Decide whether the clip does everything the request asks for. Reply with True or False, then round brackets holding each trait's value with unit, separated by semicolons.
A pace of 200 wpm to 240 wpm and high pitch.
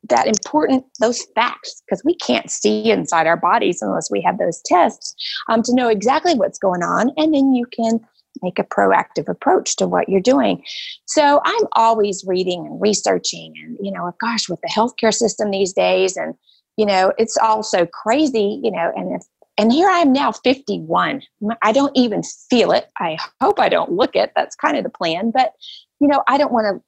True (205 wpm; 225 Hz)